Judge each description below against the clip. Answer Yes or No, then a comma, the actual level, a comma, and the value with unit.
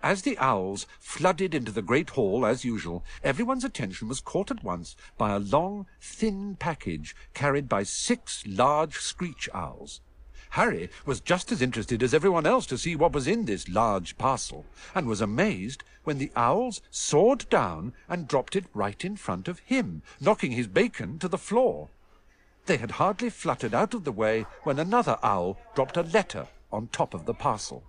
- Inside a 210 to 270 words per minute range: No, average, 180 wpm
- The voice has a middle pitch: Yes, medium, 155 Hz